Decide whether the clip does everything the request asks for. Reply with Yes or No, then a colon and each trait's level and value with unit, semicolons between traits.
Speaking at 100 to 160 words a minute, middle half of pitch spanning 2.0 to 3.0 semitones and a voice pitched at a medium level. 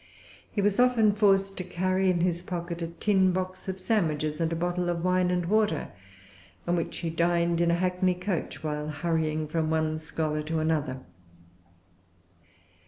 No: average, 170 wpm; narrow, 2.6 semitones; medium, 175 Hz